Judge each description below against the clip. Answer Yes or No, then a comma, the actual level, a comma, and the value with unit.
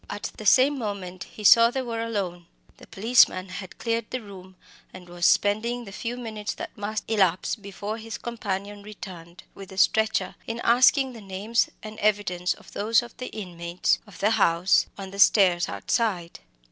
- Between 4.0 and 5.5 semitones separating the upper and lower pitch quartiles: No, average, 3.4 semitones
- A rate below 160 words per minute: No, average, 180 wpm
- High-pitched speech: Yes, high, 205 Hz